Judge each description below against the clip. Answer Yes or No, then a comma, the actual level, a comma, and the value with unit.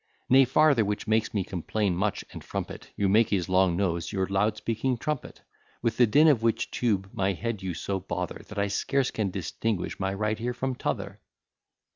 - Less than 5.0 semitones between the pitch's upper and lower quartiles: Yes, average, 3.4 semitones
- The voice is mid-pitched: No, low, 105 Hz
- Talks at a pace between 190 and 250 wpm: Yes, average, 200 wpm